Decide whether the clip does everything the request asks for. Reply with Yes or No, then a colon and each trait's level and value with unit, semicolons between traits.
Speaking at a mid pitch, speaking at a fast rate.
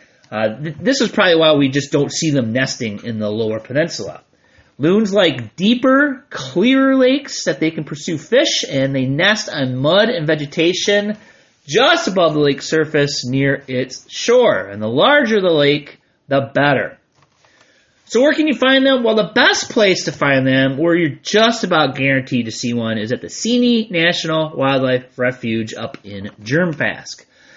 No: medium, 155 Hz; average, 170 wpm